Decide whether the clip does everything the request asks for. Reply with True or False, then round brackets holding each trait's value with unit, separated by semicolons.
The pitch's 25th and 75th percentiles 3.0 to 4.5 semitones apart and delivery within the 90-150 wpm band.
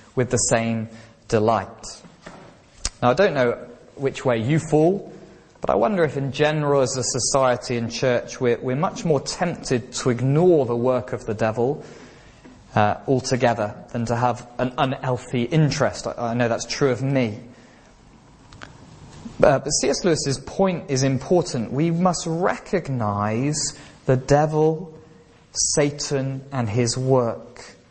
True (3.7 semitones; 140 wpm)